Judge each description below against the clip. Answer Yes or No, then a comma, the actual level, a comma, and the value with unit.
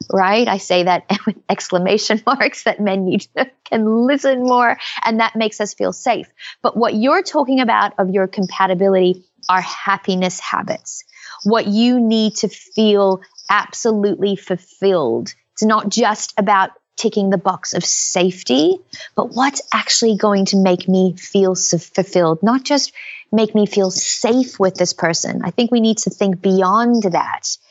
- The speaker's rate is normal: Yes, average, 160 wpm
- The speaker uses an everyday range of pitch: Yes, average, 3.3 semitones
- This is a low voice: No, high, 205 Hz